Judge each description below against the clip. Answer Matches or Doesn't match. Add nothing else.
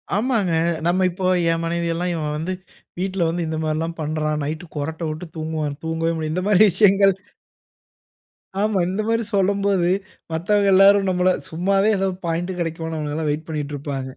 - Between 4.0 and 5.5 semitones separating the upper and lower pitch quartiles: Doesn't match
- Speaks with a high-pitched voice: Doesn't match